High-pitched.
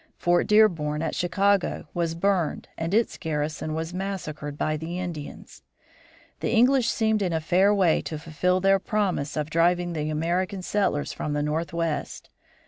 No: medium, 170 Hz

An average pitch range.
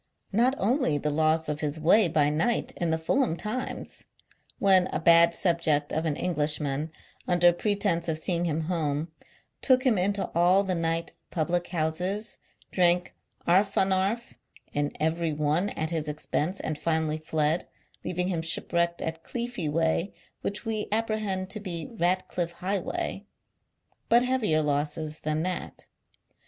Yes: average, 3.6 semitones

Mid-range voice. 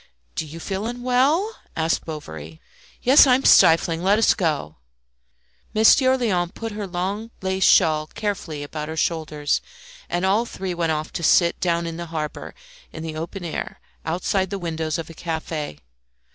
Yes: medium, 170 Hz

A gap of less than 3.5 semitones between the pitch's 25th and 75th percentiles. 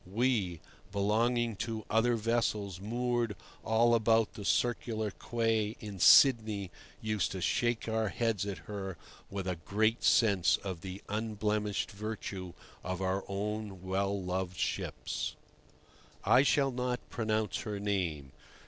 Yes: average, 2.8 semitones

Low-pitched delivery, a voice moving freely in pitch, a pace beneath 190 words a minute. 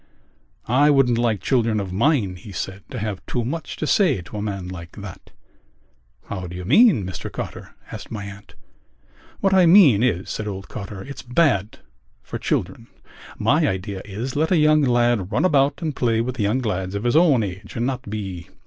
No: low, 110 Hz; wide, 5.7 semitones; average, 195 wpm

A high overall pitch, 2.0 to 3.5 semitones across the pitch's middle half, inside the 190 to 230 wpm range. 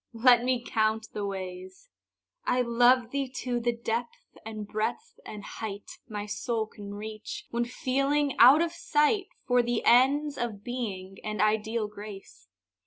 No: high, 235 Hz; average, 3.2 semitones; average, 150 wpm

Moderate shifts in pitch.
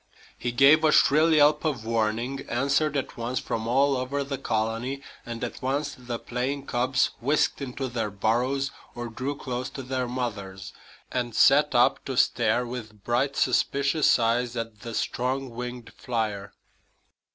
Yes: average, 3.0 semitones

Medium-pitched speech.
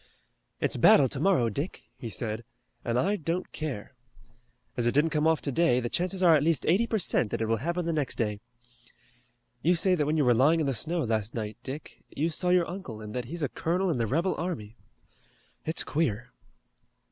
Yes: medium, 150 Hz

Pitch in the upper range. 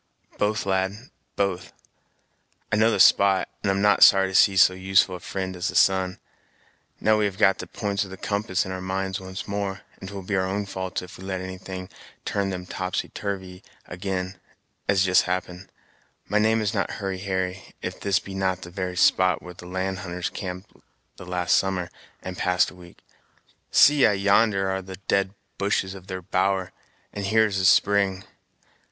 No: very low, 95 Hz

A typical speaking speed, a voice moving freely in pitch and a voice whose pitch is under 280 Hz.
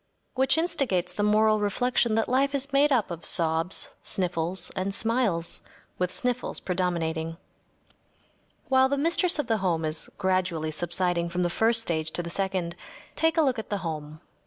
Yes: average, 165 wpm; wide, 6.6 semitones; high, 190 Hz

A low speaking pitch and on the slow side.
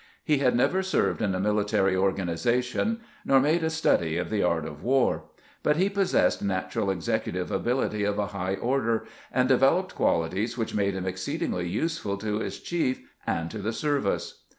No: low, 105 Hz; average, 180 wpm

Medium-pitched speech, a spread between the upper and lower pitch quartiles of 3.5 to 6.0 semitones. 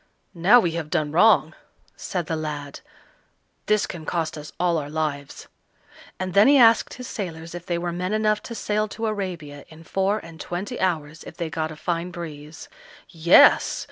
Yes: medium, 170 Hz; average, 4.1 semitones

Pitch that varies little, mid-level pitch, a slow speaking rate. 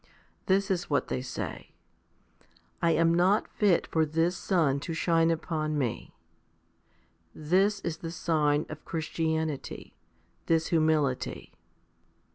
Yes: narrow, 2.0 semitones; medium, 165 Hz; slow, 120 wpm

